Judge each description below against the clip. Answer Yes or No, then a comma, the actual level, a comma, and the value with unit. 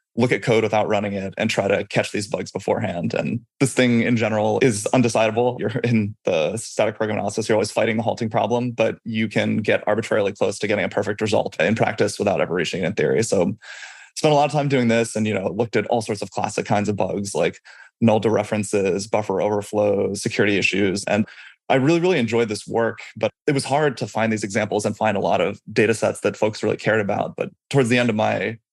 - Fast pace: Yes, fast, 235 wpm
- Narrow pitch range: Yes, narrow, 2.3 semitones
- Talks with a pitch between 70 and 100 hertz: No, low, 110 Hz